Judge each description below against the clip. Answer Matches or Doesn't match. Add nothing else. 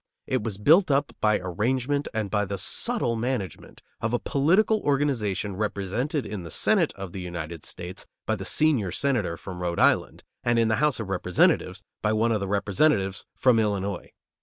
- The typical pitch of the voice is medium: Doesn't match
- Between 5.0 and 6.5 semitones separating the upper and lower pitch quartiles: Matches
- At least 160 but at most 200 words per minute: Matches